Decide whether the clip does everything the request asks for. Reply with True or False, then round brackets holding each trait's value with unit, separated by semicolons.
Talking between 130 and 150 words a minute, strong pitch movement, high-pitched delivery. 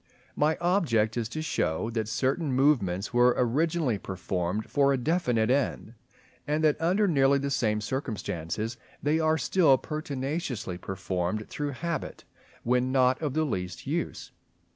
False (140 wpm; 5.8 semitones; 130 Hz)